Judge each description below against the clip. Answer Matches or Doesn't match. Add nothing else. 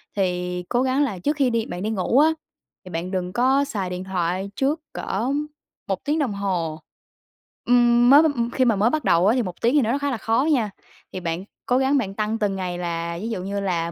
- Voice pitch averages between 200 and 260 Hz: Matches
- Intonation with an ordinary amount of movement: Doesn't match